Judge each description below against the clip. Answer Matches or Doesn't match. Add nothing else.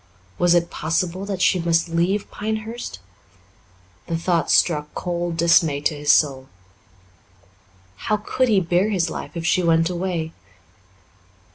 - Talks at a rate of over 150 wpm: Doesn't match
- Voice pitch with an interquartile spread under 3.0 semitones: Matches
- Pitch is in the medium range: Matches